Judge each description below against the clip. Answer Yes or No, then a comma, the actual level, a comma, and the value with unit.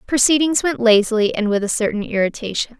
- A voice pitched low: No, high, 235 Hz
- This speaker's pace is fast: No, average, 195 wpm